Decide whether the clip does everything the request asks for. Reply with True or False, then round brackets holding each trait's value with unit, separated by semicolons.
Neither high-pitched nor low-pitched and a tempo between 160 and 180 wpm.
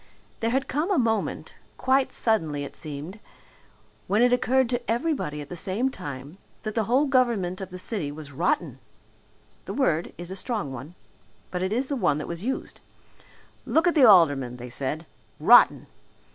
False (195 Hz; 175 wpm)